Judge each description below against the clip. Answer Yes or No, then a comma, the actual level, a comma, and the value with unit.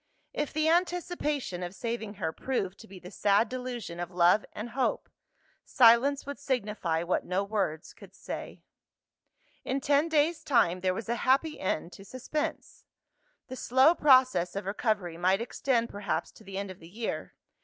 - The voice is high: Yes, high, 225 Hz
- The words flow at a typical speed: Yes, average, 165 wpm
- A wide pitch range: Yes, wide, 6.1 semitones